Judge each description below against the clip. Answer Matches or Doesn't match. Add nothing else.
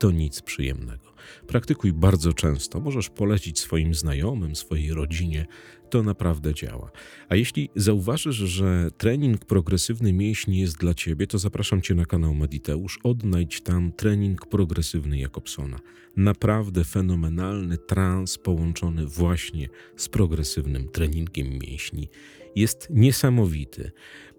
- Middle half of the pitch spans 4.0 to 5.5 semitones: Matches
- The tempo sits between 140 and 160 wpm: Doesn't match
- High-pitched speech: Doesn't match